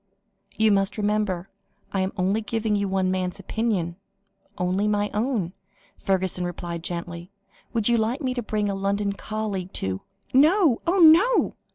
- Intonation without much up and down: No, average, 3.3 semitones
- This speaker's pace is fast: No, average, 160 wpm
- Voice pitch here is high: Yes, high, 205 Hz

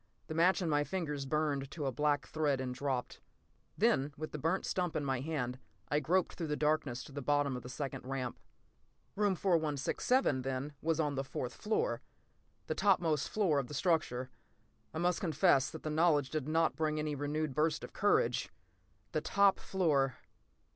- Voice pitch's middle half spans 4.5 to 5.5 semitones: No, average, 3.2 semitones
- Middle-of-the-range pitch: Yes, medium, 150 Hz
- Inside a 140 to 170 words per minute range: No, average, 180 wpm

